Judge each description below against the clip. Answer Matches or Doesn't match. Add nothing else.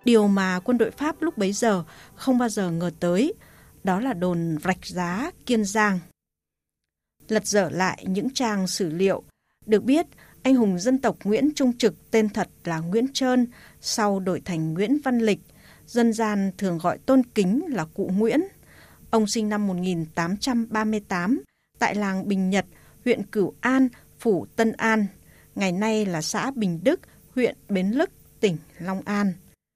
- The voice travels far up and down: Doesn't match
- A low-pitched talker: Doesn't match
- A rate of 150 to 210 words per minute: Matches